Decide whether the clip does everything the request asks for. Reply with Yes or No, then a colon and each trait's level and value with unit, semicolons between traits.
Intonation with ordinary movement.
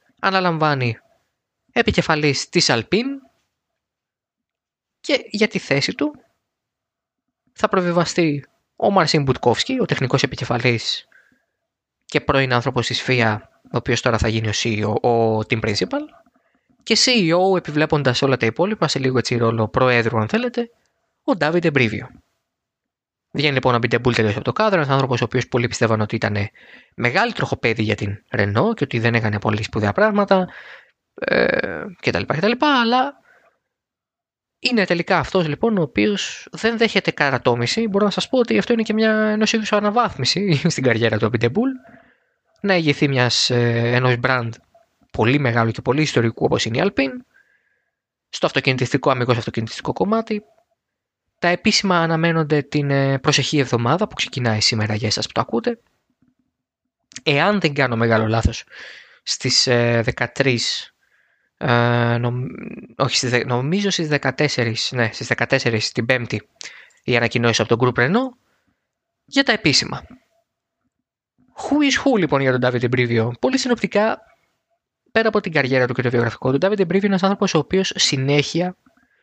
No: wide, 8.9 semitones